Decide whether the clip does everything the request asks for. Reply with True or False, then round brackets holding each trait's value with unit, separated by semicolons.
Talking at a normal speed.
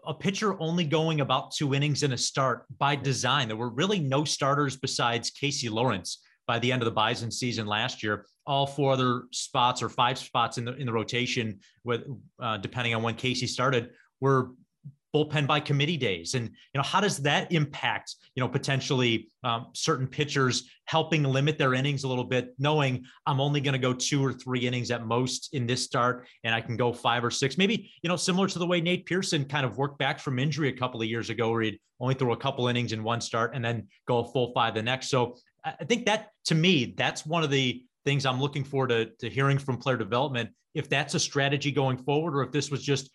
False (230 wpm)